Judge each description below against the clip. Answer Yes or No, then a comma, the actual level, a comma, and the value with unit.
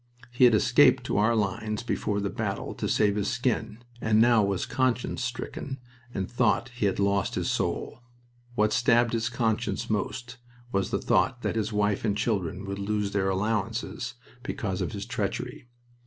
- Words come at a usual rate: Yes, average, 170 wpm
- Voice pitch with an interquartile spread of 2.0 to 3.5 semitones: Yes, average, 2.8 semitones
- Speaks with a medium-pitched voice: No, low, 110 Hz